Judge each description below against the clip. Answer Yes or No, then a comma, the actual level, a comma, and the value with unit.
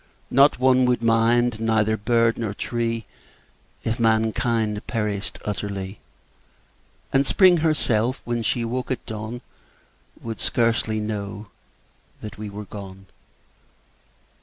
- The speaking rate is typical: No, slow, 110 wpm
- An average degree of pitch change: No, narrow, 2.2 semitones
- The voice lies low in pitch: Yes, low, 115 Hz